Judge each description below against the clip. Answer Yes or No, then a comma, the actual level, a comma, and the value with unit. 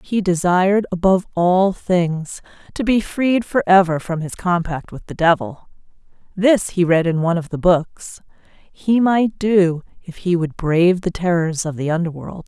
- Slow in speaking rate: No, average, 170 wpm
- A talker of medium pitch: Yes, medium, 180 Hz